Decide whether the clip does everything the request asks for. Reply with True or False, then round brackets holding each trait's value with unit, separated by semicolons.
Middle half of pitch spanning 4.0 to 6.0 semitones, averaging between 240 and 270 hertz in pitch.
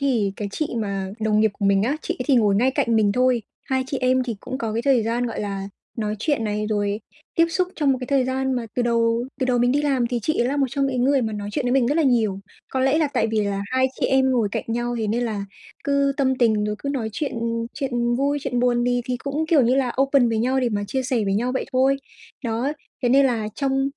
False (3.3 semitones; 245 Hz)